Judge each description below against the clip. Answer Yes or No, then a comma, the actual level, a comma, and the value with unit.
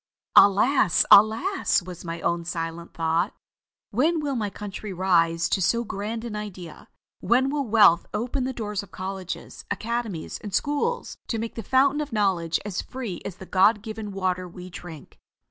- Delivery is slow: No, average, 165 wpm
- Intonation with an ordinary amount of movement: Yes, average, 4.7 semitones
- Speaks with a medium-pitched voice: No, high, 205 Hz